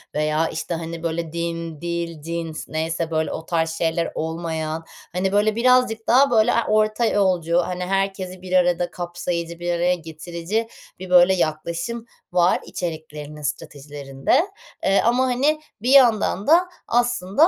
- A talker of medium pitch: Yes, medium, 175 Hz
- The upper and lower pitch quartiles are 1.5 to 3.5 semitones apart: No, average, 4.1 semitones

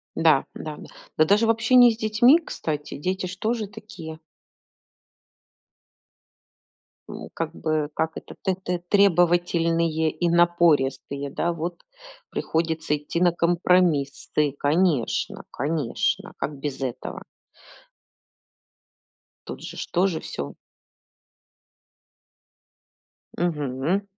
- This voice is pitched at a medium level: Yes, medium, 170 Hz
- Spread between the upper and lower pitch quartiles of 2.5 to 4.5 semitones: Yes, average, 3.5 semitones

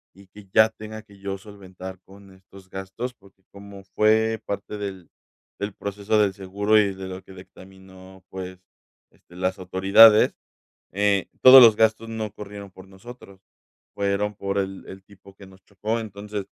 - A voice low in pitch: Yes, low, 100 Hz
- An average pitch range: No, narrow, 1.8 semitones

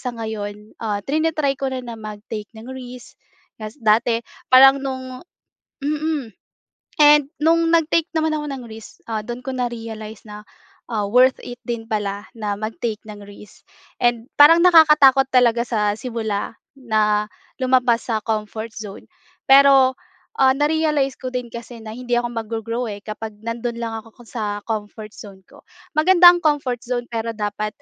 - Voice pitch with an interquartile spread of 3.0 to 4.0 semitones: Yes, average, 3.7 semitones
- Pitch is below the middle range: No, high, 235 Hz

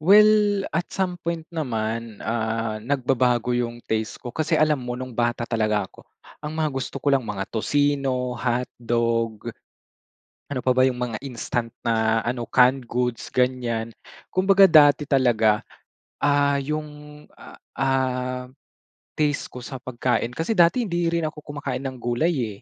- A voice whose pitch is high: No, low, 130 Hz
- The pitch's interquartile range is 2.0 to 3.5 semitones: No, average, 4.0 semitones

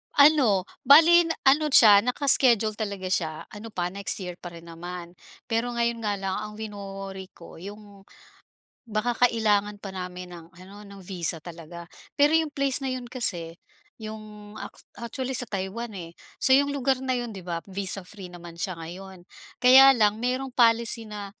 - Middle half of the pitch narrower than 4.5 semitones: No, average, 4.8 semitones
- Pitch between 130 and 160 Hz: No, high, 210 Hz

